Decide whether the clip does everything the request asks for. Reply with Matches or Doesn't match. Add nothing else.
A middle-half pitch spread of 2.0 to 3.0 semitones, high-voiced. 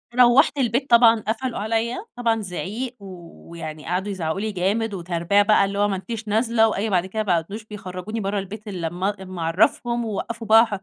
Doesn't match